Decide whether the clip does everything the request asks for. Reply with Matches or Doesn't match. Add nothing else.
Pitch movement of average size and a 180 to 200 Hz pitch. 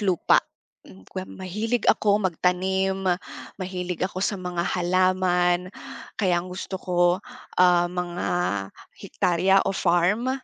Doesn't match